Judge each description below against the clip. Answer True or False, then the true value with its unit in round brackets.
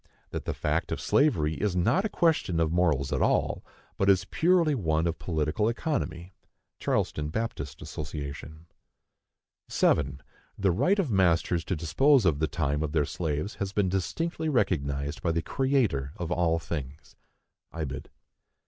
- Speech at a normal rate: True (150 wpm)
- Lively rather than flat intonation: True (5.7 semitones)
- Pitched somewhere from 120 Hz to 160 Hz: False (85 Hz)